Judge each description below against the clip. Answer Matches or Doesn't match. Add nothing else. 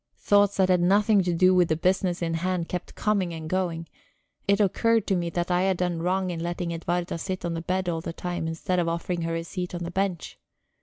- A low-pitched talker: Doesn't match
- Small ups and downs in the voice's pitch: Matches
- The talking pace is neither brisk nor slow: Doesn't match